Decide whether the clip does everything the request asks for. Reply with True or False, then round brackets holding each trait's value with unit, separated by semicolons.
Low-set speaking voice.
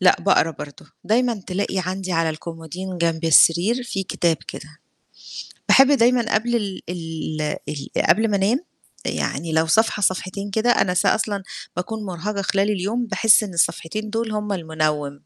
False (190 Hz)